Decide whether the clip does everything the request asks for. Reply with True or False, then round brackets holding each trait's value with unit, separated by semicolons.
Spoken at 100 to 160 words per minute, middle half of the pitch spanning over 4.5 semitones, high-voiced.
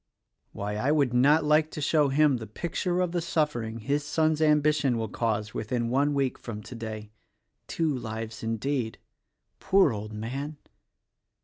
False (150 wpm; 5.2 semitones; 135 Hz)